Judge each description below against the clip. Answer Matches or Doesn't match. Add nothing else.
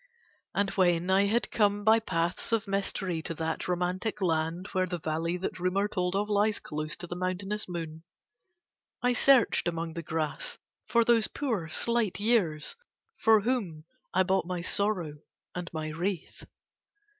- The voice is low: Doesn't match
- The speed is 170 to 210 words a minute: Doesn't match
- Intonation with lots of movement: Doesn't match